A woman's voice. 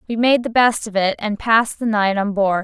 Yes: female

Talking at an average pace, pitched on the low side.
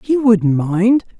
No: average, 150 wpm; high, 210 Hz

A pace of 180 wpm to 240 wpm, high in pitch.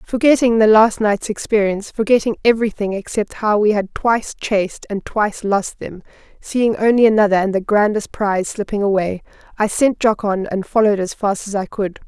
Yes: average, 185 wpm; high, 210 Hz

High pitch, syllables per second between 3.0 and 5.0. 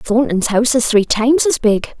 No: high, 235 Hz; 5.2 syllables/s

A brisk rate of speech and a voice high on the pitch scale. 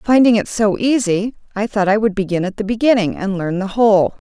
Yes: fast, 225 wpm; high, 210 Hz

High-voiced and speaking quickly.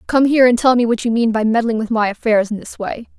Yes: high, 230 Hz; fast, 300 wpm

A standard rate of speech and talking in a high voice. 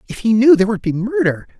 No: fast, 265 wpm; high, 200 Hz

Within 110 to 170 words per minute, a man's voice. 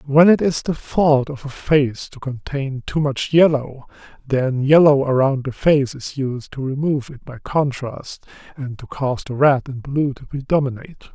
No: average, 185 wpm; male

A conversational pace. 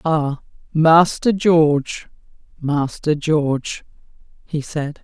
No: slow, 85 wpm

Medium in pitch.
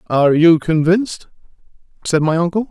Yes: medium, 170 Hz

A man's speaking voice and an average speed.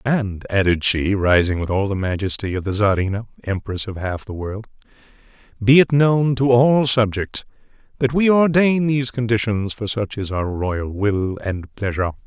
Yes: male; average, 170 wpm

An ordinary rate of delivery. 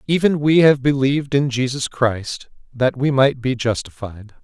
Yes: average, 160 wpm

